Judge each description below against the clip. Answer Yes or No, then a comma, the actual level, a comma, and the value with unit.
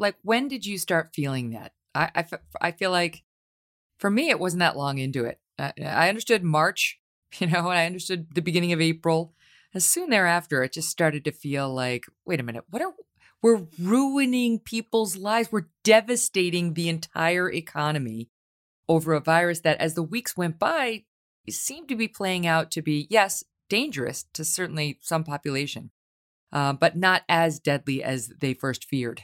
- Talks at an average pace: Yes, average, 180 wpm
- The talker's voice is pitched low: No, medium, 165 Hz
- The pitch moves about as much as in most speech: No, wide, 5.8 semitones